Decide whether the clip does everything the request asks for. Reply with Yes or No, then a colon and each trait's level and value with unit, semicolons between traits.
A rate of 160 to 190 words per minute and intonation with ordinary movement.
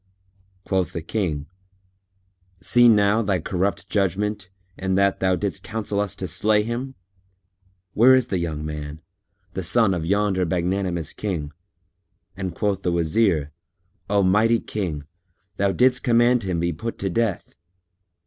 No: average, 140 wpm; average, 3.6 semitones